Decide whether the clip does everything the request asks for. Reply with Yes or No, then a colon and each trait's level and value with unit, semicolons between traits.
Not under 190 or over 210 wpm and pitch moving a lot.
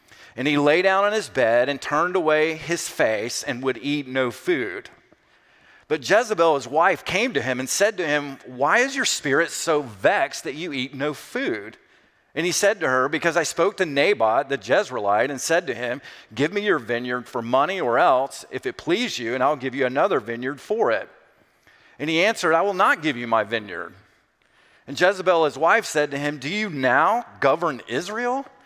Yes: fast, 205 wpm; wide, 6.2 semitones